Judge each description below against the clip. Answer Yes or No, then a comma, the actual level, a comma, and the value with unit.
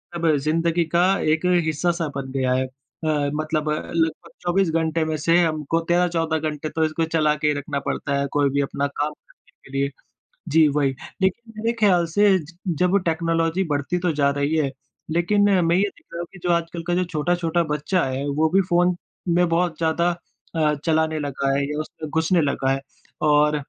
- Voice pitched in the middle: Yes, medium, 160 Hz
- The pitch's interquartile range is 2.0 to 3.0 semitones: Yes, narrow, 2.6 semitones